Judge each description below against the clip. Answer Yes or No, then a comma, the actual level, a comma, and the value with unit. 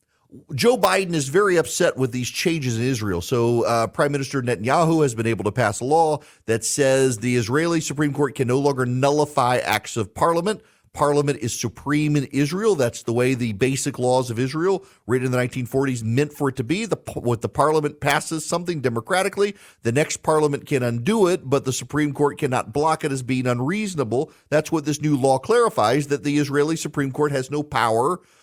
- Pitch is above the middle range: No, medium, 140 Hz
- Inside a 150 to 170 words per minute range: No, average, 200 wpm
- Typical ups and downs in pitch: Yes, average, 3.6 semitones